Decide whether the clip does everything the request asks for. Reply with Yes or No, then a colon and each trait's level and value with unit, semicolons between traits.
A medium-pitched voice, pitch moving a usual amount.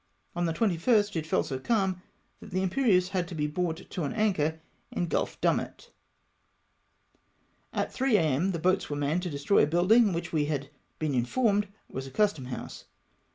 Yes: medium, 175 Hz; average, 5.0 semitones